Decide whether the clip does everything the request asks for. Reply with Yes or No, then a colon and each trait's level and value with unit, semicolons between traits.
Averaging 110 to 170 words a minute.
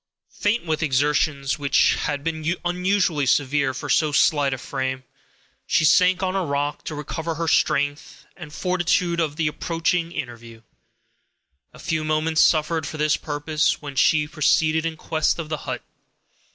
Yes: average, 160 wpm